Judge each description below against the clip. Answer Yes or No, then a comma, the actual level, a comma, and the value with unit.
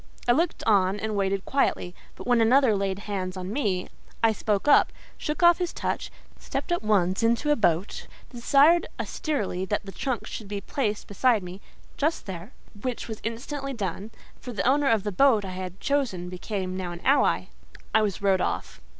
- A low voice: No, high, 210 Hz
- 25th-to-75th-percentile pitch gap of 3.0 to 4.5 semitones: No, wide, 5.5 semitones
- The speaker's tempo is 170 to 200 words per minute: Yes, average, 180 wpm